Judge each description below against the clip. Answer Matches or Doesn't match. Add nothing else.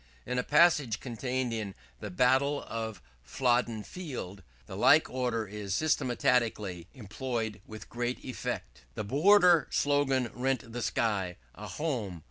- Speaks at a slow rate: Matches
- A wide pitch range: Doesn't match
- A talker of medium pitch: Doesn't match